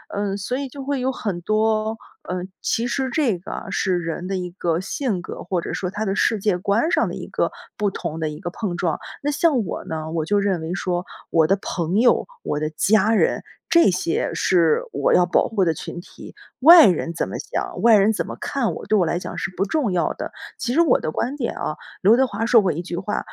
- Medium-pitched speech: No, high, 195 Hz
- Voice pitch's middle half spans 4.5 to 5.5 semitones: Yes, average, 4.8 semitones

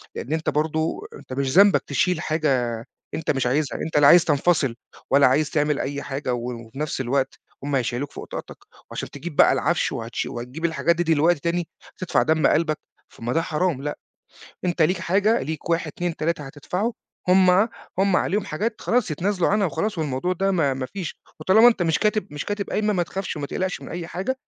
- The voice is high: No, medium, 160 Hz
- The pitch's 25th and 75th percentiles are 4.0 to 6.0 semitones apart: Yes, average, 4.5 semitones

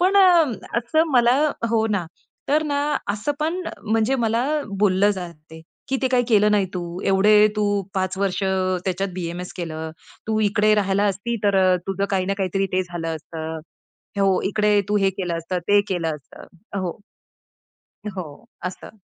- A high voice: Yes, high, 195 Hz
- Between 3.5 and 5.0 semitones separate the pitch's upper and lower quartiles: No, average, 2.8 semitones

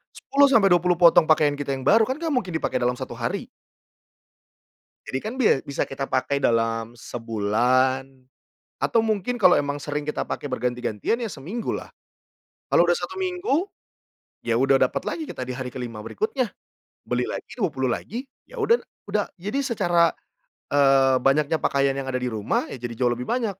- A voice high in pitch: No, medium, 145 Hz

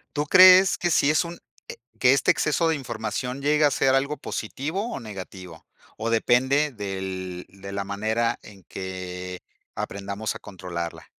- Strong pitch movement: Yes, wide, 7.0 semitones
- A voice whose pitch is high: No, low, 110 Hz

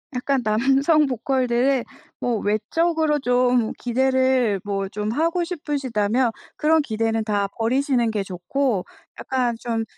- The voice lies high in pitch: Yes, very high, 250 Hz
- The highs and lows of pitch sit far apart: No, average, 3.7 semitones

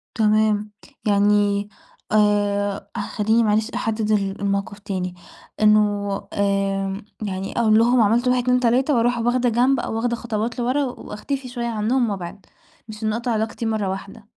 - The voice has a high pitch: Yes, high, 215 Hz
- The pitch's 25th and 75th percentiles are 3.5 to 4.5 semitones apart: No, average, 2.8 semitones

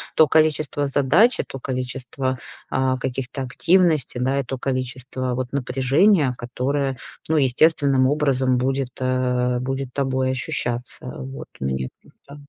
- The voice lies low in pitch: Yes, low, 130 Hz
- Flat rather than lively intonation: Yes, narrow, 1.8 semitones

